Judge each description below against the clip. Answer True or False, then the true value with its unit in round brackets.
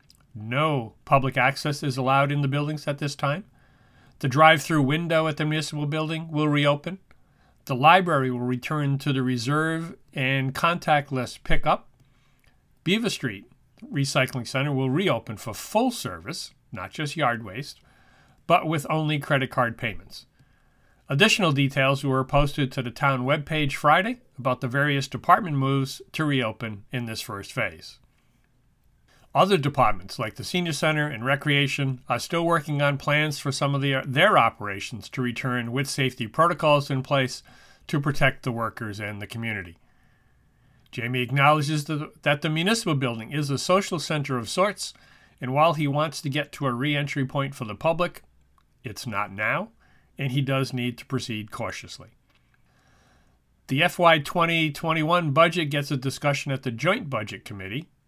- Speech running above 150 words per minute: True (160 wpm)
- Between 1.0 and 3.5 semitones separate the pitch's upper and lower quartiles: True (3.2 semitones)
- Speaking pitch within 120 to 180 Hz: True (140 Hz)